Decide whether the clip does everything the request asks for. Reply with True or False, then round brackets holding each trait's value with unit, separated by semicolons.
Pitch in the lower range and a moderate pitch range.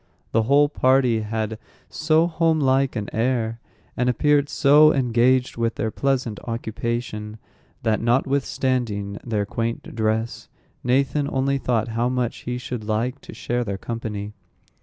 True (120 Hz; 3.2 semitones)